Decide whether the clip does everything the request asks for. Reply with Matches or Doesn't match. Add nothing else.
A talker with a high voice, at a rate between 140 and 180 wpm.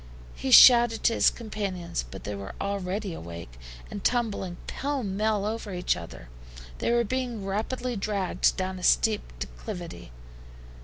Matches